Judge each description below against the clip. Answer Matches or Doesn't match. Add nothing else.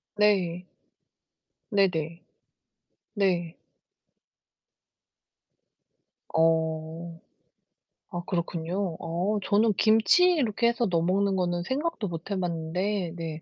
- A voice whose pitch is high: Doesn't match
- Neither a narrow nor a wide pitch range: Matches